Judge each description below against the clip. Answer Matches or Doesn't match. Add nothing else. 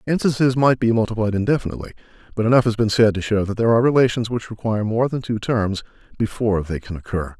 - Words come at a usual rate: Doesn't match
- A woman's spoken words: Doesn't match